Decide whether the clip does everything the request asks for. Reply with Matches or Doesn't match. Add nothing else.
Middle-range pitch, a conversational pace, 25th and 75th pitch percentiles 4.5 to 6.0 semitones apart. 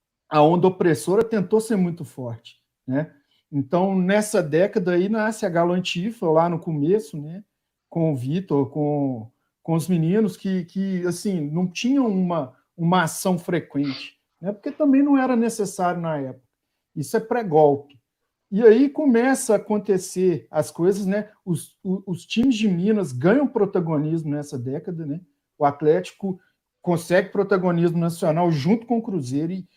Matches